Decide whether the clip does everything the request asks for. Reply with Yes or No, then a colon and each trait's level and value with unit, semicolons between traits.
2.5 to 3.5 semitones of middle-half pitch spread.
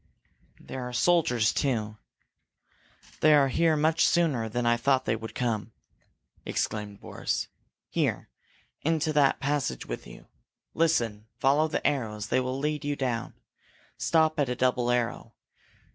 No: average, 4.5 semitones